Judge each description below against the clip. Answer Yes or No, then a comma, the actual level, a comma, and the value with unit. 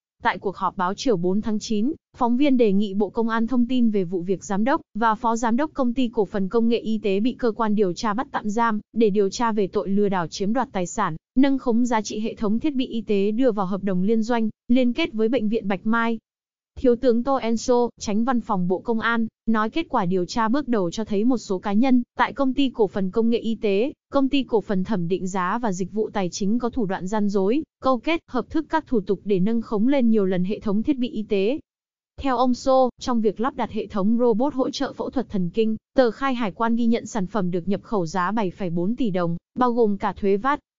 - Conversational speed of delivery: No, fast, 265 wpm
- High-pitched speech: Yes, high, 225 Hz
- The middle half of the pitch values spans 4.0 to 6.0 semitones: No, average, 3.4 semitones